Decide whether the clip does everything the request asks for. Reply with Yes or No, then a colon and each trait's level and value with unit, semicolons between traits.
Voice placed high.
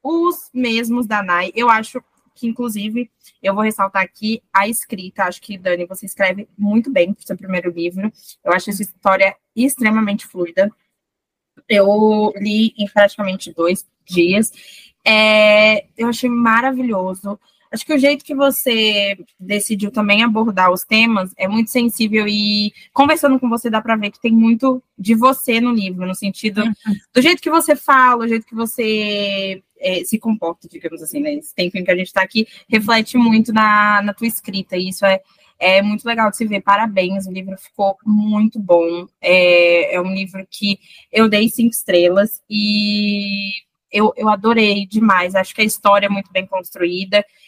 Yes: high, 210 Hz